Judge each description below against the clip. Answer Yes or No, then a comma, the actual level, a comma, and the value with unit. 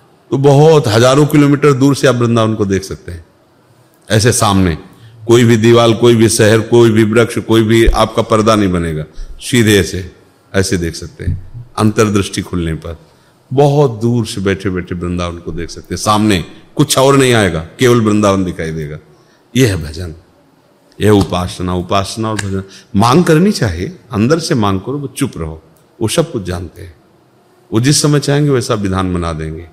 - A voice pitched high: No, low, 105 Hz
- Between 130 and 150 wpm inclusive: No, average, 180 wpm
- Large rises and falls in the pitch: No, average, 5.0 semitones